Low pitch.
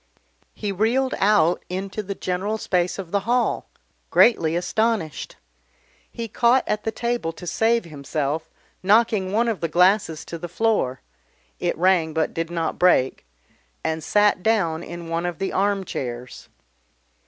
No: medium, 185 Hz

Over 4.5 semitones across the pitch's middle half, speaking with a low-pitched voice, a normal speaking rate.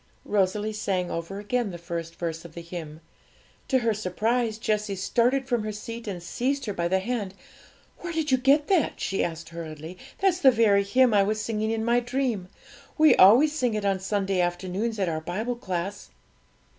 No: average, 4.9 semitones; high, 210 Hz; average, 190 wpm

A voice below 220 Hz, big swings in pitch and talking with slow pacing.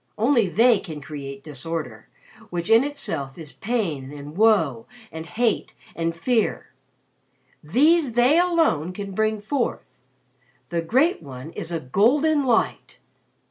Yes: high, 190 Hz; wide, 8.1 semitones; slow, 130 wpm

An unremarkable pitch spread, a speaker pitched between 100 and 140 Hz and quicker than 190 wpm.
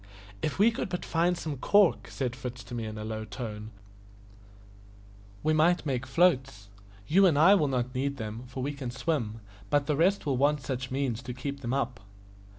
Yes: average, 4.2 semitones; low, 135 Hz; average, 200 wpm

